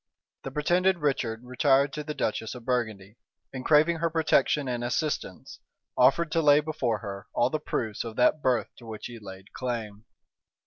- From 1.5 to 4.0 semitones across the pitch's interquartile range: No, average, 4.9 semitones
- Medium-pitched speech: No, low, 130 Hz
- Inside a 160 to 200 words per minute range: Yes, average, 175 wpm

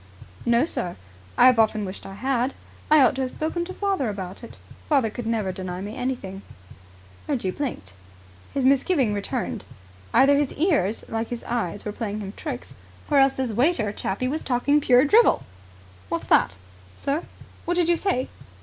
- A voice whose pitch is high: Yes, very high, 250 Hz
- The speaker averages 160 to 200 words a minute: Yes, average, 175 wpm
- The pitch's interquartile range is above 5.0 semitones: Yes, wide, 5.4 semitones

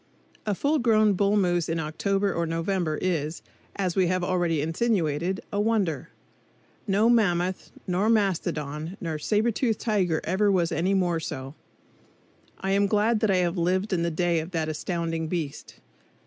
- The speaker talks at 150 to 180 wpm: Yes, average, 160 wpm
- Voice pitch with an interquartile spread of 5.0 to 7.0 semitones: No, average, 3.6 semitones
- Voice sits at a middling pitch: Yes, medium, 180 Hz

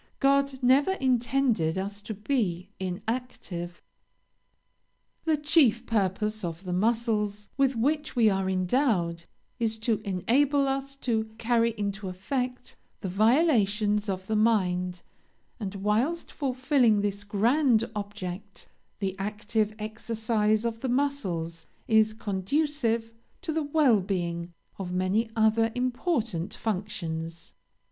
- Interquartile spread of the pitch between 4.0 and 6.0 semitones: Yes, average, 4.6 semitones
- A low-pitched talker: No, high, 220 Hz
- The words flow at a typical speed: No, slow, 115 wpm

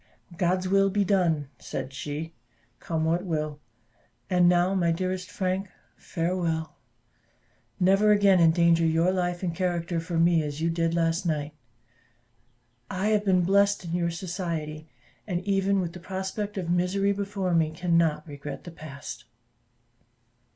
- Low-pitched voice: No, medium, 175 Hz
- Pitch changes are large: No, narrow, 2.4 semitones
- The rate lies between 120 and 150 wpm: Yes, average, 145 wpm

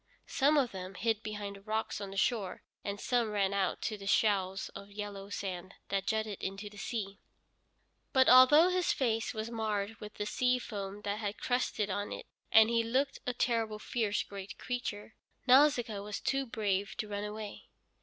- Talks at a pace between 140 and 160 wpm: No, average, 185 wpm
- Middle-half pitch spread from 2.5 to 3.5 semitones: Yes, average, 2.8 semitones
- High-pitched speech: Yes, high, 210 Hz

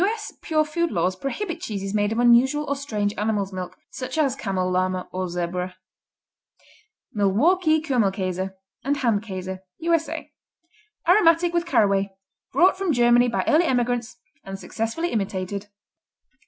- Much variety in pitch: Yes, wide, 8.2 semitones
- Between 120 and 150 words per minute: Yes, slow, 135 wpm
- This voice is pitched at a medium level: No, high, 235 Hz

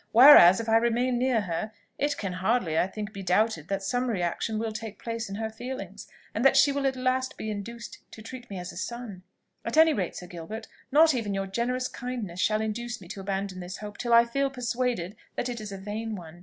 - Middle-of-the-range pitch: No, high, 220 Hz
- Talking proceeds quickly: Yes, fast, 230 wpm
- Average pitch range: Yes, average, 4.1 semitones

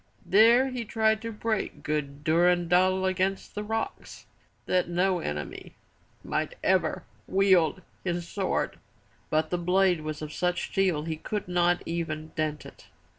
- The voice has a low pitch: No, medium, 180 Hz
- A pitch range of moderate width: Yes, average, 3.5 semitones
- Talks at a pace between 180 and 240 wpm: No, average, 140 wpm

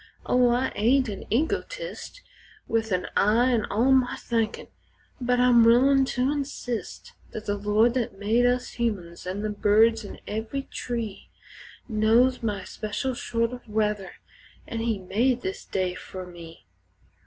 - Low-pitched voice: No, high, 230 Hz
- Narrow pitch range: No, average, 3.2 semitones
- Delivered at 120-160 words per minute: Yes, average, 150 wpm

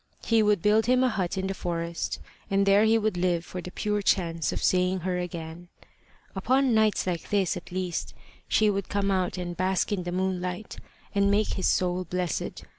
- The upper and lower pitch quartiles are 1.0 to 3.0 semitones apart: Yes, narrow, 2.6 semitones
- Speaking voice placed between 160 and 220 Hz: Yes, medium, 185 Hz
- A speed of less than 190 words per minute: No, average, 195 wpm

